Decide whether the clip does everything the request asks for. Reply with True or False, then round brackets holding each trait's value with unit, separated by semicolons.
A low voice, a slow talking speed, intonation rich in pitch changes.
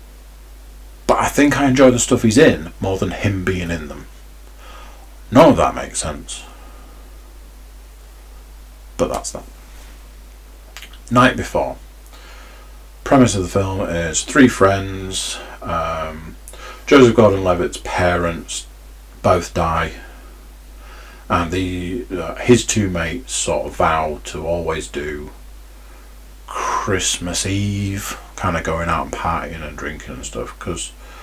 True (85 Hz; 120 wpm; 7.0 semitones)